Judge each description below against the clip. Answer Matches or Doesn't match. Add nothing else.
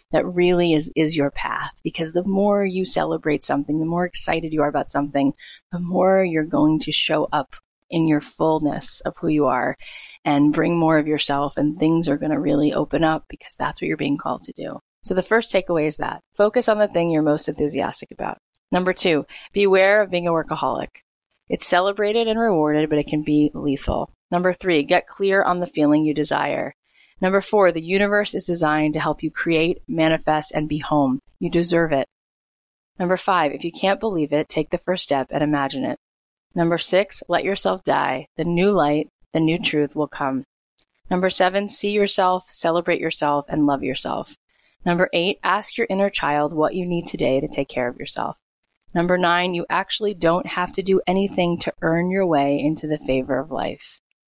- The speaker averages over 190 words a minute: Matches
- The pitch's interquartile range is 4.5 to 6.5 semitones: Doesn't match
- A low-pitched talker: Doesn't match